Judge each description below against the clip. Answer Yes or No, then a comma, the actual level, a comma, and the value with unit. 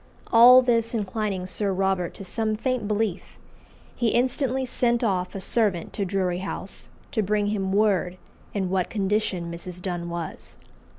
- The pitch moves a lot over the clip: No, average, 3.4 semitones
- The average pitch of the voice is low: No, high, 200 Hz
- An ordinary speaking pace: Yes, average, 155 wpm